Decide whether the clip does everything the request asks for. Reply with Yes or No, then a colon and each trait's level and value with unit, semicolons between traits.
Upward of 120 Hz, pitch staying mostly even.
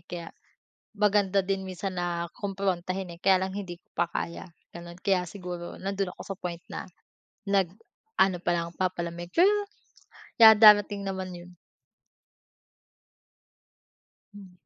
Yes: medium, 185 Hz; narrow, 2.2 semitones